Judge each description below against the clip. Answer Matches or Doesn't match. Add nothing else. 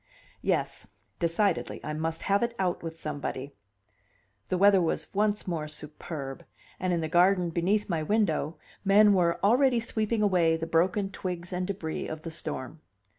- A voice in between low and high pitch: Matches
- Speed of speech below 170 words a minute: Matches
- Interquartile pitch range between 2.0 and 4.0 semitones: Matches